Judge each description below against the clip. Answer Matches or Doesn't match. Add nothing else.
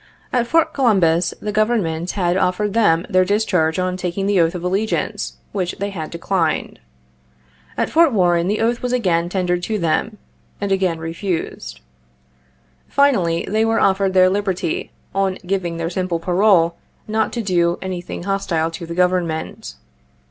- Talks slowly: Doesn't match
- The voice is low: Doesn't match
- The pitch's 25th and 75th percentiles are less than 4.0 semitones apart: Matches